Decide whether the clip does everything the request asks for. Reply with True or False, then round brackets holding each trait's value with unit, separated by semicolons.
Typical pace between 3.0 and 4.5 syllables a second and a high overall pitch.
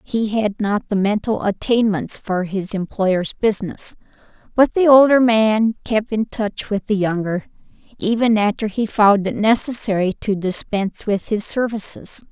True (4.4 syllables/s; 210 Hz)